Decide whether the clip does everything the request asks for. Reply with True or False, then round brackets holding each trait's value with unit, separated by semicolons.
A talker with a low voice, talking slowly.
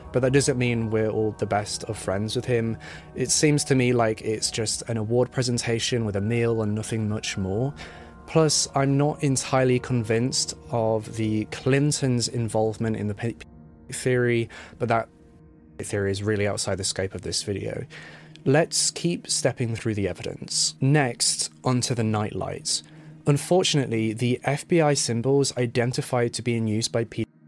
False (115 Hz; 165 wpm)